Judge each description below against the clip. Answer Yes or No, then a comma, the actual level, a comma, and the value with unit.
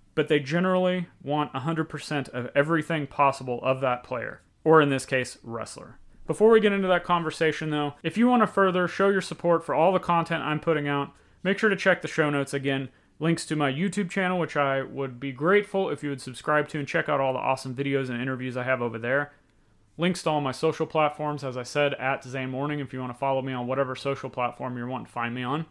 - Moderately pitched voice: Yes, medium, 145 Hz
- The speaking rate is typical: No, fast, 240 wpm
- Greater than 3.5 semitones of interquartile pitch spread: Yes, average, 3.9 semitones